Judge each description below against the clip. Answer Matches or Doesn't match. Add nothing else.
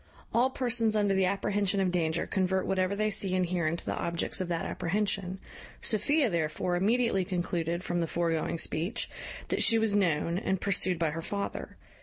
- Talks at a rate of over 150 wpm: Matches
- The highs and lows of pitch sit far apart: Doesn't match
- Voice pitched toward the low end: Doesn't match